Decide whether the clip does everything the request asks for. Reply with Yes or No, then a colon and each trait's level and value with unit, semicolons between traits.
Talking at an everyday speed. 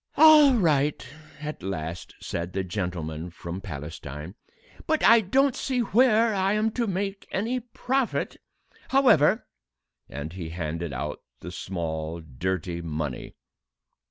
No: slow, 130 wpm